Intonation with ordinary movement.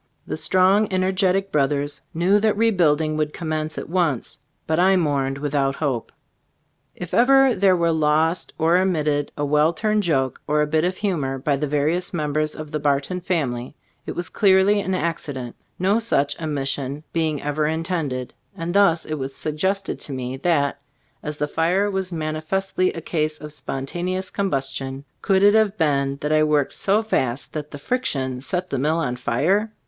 Yes: average, 4.4 semitones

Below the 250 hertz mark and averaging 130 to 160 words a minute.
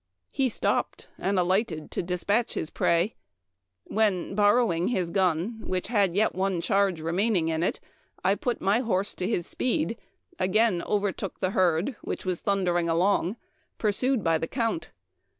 Yes: high, 190 Hz; average, 150 wpm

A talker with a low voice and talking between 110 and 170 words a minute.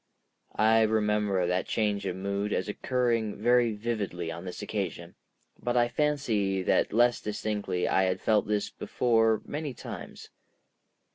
Yes: low, 105 Hz; average, 140 wpm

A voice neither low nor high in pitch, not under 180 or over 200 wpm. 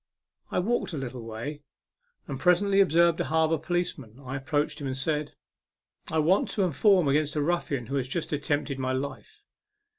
Yes: medium, 150 Hz; average, 185 wpm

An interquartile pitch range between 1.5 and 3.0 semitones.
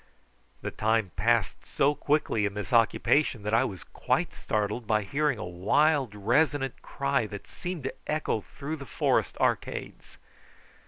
No: wide, 5.6 semitones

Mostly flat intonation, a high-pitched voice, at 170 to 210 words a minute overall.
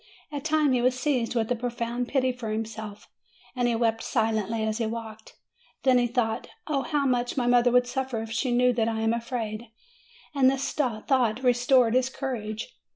Yes: narrow, 2.3 semitones; high, 245 Hz; average, 190 wpm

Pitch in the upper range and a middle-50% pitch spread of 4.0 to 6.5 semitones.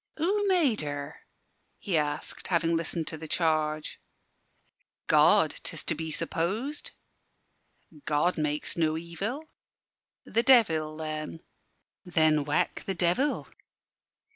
No: medium, 165 Hz; average, 4.9 semitones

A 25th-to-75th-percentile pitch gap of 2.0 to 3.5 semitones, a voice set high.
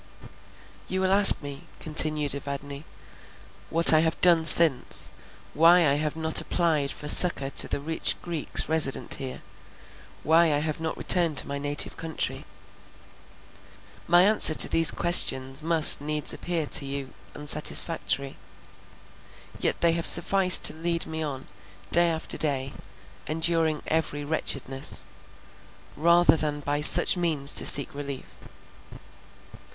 No: average, 2.7 semitones; medium, 155 Hz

